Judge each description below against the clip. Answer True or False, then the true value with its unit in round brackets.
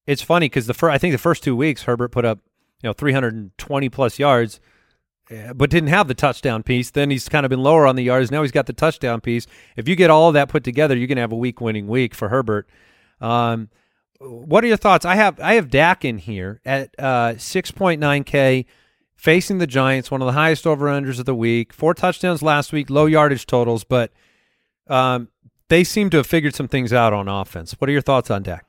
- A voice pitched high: False (135 Hz)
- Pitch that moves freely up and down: False (4.4 semitones)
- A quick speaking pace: True (225 wpm)